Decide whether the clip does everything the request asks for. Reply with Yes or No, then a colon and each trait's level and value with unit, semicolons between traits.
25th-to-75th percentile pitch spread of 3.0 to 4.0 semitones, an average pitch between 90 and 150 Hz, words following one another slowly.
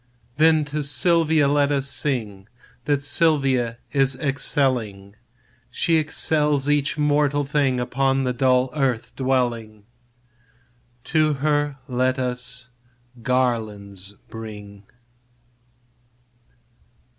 Yes: average, 3.3 semitones; low, 135 Hz; slow, 90 wpm